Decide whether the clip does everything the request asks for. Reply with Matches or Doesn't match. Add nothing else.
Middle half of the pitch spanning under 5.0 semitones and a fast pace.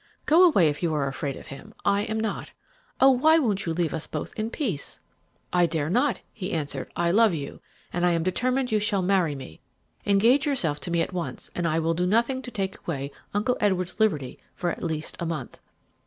Doesn't match